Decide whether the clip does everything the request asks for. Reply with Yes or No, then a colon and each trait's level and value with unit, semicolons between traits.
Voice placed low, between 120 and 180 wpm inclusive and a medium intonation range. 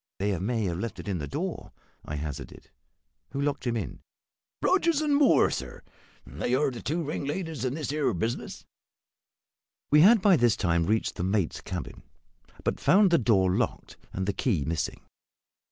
No: low, 120 Hz; average, 170 wpm; wide, 8.6 semitones